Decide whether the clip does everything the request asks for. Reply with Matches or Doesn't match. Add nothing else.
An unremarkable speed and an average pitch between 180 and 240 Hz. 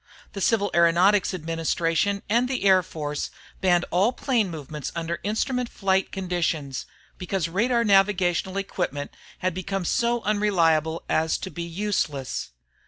Doesn't match